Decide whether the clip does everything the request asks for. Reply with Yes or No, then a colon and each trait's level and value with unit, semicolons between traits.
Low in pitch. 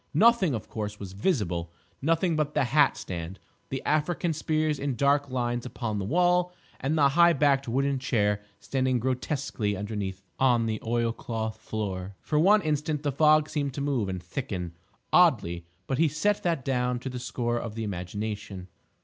Yes: low, 130 Hz